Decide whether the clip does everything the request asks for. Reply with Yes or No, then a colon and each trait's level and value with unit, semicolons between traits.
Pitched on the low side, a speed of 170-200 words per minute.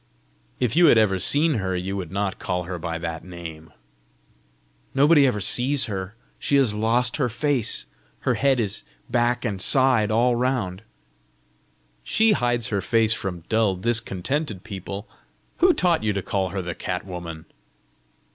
No: low, 110 Hz; average, 155 wpm